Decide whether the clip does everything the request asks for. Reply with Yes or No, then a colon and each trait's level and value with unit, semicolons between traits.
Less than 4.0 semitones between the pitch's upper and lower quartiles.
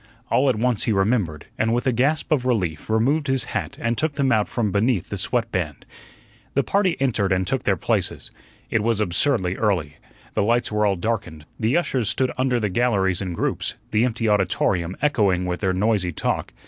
No: average, 4.8 semitones